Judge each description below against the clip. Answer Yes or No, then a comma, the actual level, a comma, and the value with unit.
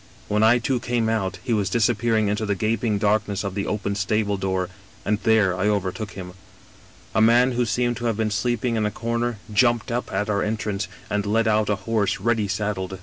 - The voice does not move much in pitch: Yes, narrow, 2.3 semitones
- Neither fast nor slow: No, fast, 210 wpm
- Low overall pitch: Yes, low, 105 Hz